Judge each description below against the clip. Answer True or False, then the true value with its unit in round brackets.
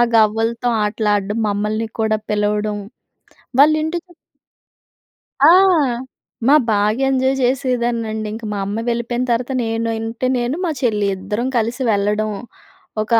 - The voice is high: True (225 Hz)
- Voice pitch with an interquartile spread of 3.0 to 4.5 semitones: False (2.5 semitones)